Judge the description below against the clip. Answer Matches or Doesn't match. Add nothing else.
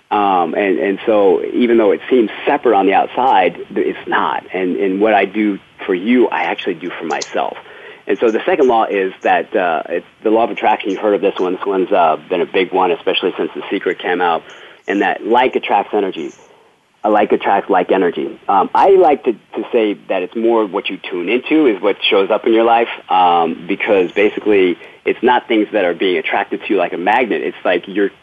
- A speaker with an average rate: Doesn't match